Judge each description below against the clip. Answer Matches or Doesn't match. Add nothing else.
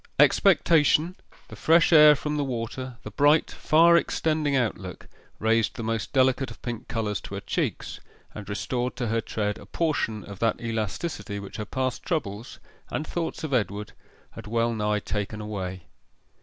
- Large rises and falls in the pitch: Matches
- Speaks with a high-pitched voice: Doesn't match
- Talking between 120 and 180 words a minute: Matches